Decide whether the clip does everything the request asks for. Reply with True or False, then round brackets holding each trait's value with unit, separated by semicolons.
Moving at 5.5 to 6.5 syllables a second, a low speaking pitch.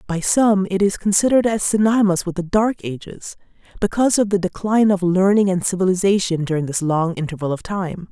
False (5.9 syllables/s; 190 Hz)